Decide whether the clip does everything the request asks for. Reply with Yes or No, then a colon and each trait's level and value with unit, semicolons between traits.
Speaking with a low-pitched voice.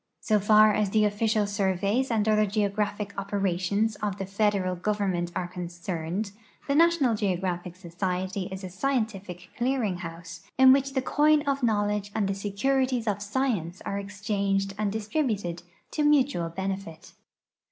No: high, 205 Hz